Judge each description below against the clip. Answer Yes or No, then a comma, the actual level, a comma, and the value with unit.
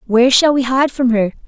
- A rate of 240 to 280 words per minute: Yes, fast, 245 wpm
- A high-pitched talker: Yes, very high, 250 Hz